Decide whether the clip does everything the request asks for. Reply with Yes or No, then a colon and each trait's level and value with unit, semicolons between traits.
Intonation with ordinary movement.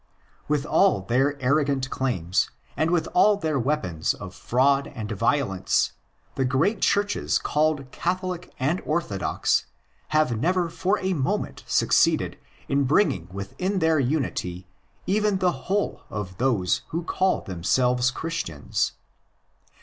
No: wide, 6.0 semitones